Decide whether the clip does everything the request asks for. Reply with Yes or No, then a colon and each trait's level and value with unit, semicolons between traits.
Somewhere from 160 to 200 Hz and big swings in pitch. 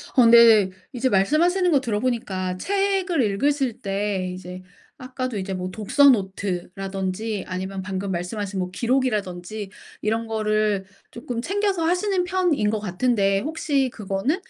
No: high, 215 Hz; wide, 5.8 semitones